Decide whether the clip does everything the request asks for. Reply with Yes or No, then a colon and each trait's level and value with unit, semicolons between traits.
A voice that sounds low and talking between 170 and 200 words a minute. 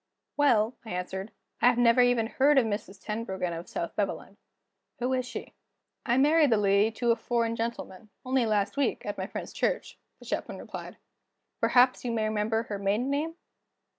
No: high, 230 Hz; average, 175 wpm